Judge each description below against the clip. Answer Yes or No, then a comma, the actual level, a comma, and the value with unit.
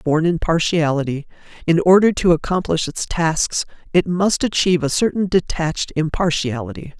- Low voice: No, medium, 165 Hz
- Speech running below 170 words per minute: Yes, slow, 135 wpm